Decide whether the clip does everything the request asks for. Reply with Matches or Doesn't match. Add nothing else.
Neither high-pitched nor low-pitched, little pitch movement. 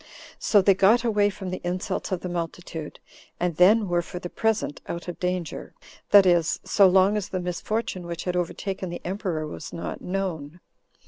Matches